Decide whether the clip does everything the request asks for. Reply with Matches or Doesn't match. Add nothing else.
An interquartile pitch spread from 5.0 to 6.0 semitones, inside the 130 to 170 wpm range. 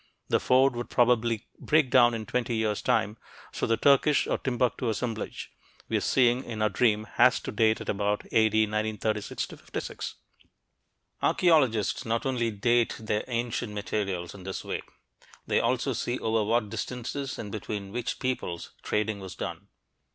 Doesn't match